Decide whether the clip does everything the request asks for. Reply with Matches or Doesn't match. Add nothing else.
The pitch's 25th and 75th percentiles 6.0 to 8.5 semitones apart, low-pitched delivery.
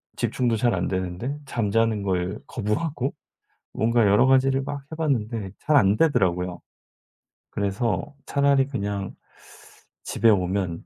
Doesn't match